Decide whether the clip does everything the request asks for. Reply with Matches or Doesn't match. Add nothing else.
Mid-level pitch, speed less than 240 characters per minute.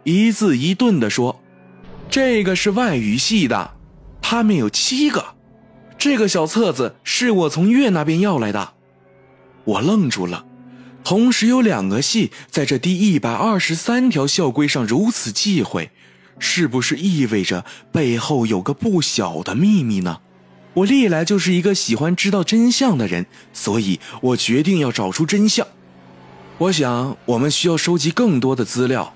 Matches